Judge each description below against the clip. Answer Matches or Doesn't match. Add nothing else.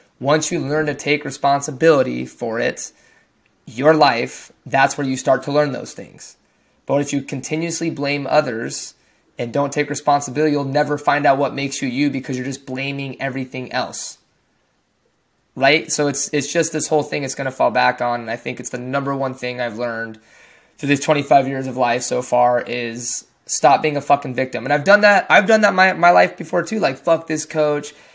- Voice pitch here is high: Doesn't match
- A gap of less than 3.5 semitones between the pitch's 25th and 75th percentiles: Matches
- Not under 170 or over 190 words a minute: Doesn't match